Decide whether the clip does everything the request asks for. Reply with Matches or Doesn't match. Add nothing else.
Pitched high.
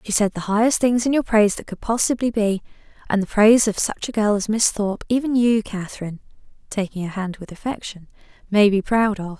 Matches